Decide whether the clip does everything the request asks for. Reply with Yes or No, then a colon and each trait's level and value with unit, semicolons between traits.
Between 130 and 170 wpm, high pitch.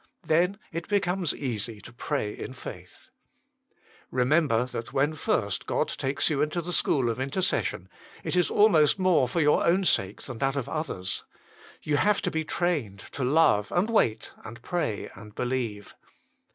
No: average, 165 wpm; medium, 140 Hz